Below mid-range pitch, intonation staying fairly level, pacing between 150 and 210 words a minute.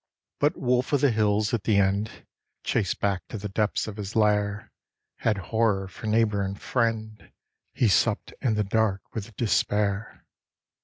Yes: low, 105 Hz; narrow, 1.9 semitones; average, 160 wpm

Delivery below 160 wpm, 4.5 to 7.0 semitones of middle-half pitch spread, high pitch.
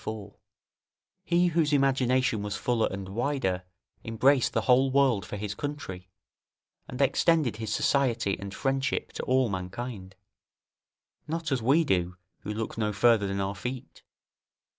No: average, 140 wpm; average, 5.2 semitones; low, 120 Hz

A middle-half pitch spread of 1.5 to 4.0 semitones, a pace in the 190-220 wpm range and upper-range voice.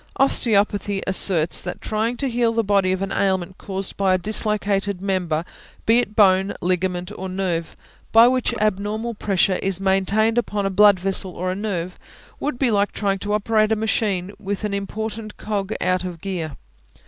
No: narrow, 2.4 semitones; average, 180 wpm; high, 200 Hz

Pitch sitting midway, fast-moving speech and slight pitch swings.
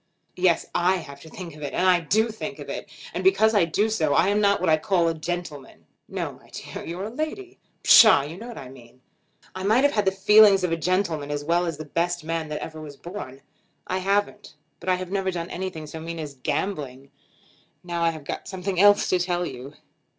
No: medium, 175 Hz; fast, 230 wpm; average, 4.0 semitones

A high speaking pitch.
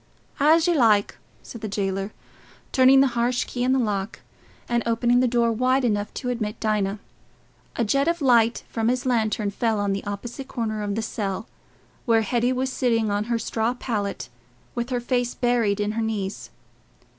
Yes: high, 230 Hz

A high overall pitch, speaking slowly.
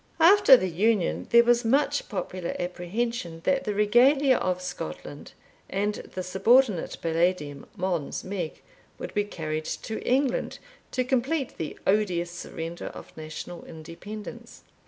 Yes: high, 195 Hz; slow, 130 wpm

